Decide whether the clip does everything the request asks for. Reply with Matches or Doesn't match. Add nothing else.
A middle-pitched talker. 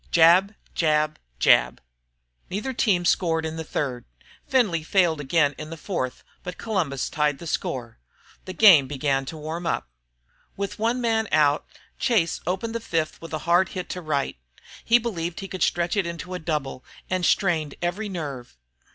Matches